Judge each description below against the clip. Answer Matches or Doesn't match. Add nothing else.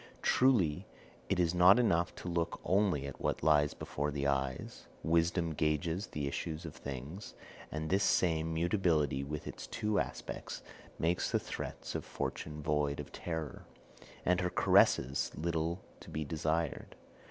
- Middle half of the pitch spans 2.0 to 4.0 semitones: Matches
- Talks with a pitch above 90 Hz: Doesn't match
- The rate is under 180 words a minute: Matches